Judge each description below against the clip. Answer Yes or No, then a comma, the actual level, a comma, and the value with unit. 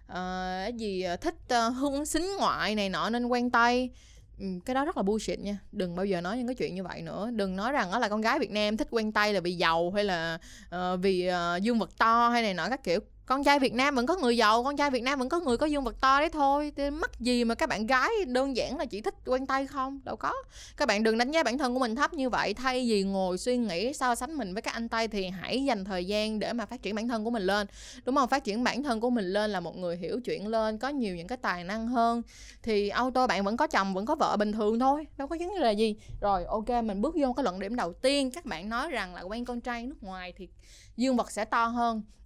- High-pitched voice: Yes, high, 235 Hz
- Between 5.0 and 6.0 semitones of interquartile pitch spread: No, average, 4.3 semitones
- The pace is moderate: No, fast, 285 wpm